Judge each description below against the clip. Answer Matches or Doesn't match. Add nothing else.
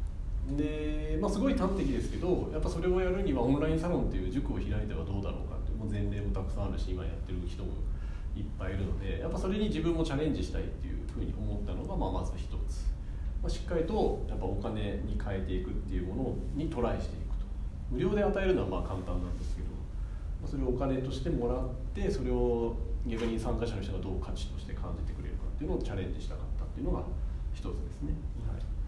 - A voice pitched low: Matches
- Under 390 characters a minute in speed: Doesn't match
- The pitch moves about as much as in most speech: Doesn't match